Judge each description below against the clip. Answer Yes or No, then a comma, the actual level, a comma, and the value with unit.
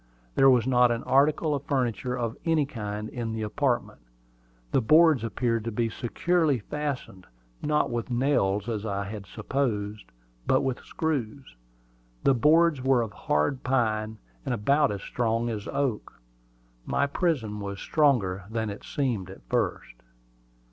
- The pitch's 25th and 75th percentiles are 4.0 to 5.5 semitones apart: Yes, average, 4.6 semitones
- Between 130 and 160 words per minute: Yes, average, 150 wpm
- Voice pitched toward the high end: No, low, 120 Hz